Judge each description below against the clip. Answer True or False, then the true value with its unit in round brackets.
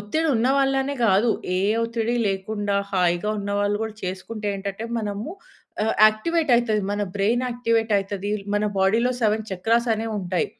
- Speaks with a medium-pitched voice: False (215 Hz)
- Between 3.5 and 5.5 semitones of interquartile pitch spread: False (2.6 semitones)